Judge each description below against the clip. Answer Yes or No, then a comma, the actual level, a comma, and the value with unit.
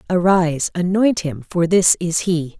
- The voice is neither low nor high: Yes, medium, 175 Hz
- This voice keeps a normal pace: Yes, average, 160 wpm